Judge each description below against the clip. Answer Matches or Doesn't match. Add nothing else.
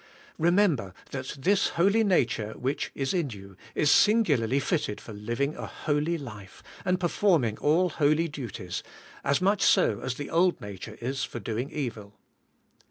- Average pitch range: Doesn't match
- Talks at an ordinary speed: Matches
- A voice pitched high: Doesn't match